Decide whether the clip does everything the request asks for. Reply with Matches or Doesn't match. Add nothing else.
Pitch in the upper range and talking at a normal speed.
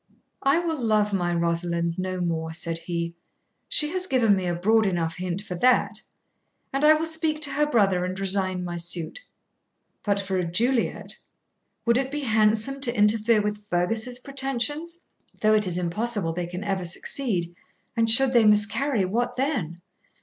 Matches